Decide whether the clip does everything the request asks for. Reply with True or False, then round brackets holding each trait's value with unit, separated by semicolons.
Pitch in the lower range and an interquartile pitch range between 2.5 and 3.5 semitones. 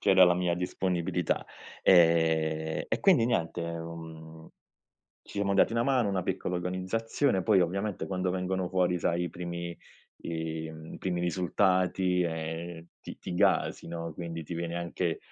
False (90 Hz; 2.0 semitones)